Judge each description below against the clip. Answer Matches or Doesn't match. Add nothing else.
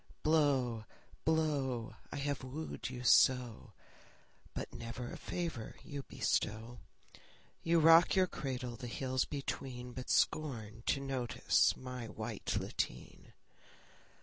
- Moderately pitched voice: Doesn't match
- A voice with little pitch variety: Doesn't match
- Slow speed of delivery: Matches